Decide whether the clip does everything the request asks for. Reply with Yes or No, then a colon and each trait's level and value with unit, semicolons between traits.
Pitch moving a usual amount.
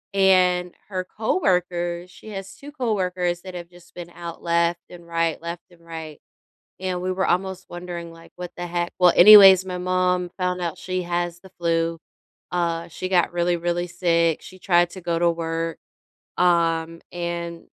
No: narrow, 1.3 semitones